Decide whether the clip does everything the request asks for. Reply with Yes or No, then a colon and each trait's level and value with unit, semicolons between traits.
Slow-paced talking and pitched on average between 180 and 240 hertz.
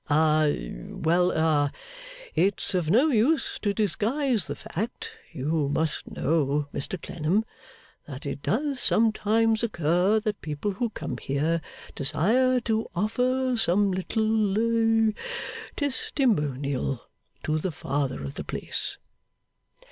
Yes: slow, 115 wpm; high, 190 Hz